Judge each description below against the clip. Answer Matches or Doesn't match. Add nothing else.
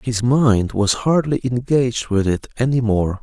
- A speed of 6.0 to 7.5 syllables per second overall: Doesn't match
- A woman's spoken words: Doesn't match